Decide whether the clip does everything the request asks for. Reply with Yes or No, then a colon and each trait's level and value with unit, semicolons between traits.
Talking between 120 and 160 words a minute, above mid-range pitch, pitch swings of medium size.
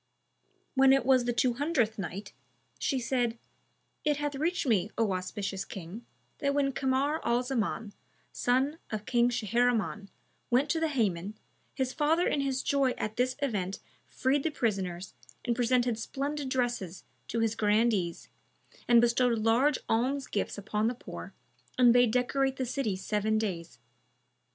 Yes: average, 150 wpm; high, 240 Hz; average, 4.0 semitones